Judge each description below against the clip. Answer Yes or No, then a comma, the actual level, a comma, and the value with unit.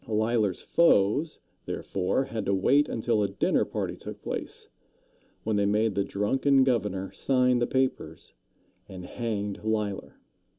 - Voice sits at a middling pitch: No, low, 110 Hz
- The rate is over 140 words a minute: No, slow, 135 wpm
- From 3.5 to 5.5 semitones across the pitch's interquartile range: Yes, average, 4.1 semitones